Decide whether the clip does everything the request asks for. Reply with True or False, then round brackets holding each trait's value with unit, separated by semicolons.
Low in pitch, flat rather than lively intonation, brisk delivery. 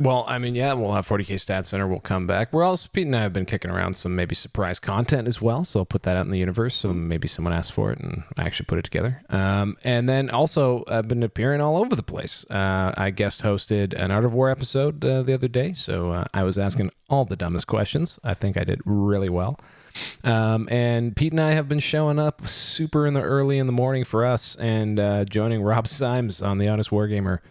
False (110 Hz; 5.1 semitones; 245 wpm)